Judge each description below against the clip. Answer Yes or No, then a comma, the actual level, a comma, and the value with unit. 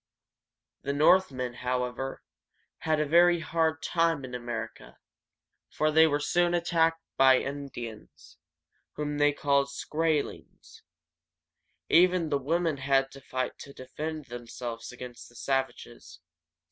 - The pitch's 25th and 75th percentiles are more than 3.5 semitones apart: Yes, average, 4.1 semitones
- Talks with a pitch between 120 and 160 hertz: Yes, medium, 140 Hz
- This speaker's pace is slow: Yes, slow, 120 wpm